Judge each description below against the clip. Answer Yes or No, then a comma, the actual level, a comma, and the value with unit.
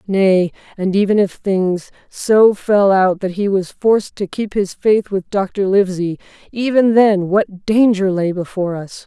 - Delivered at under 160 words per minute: No, average, 170 wpm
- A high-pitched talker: Yes, high, 195 Hz